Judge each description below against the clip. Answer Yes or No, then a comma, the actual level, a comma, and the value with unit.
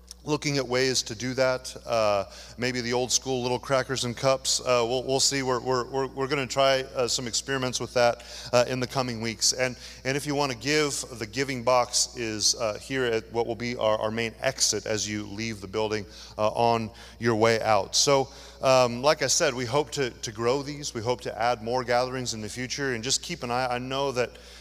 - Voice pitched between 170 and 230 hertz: No, low, 125 Hz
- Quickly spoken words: Yes, fast, 230 wpm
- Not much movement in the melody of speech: Yes, narrow, 2.3 semitones